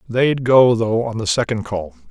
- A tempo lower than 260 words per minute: Yes, average, 200 wpm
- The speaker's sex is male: Yes, male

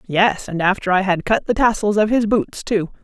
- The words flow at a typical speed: No, fast, 235 wpm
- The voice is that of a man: No, female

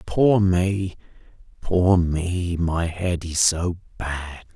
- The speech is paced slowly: Yes, slow, 120 wpm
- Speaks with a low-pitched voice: Yes, very low, 90 Hz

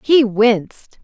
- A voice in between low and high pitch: No, high, 230 Hz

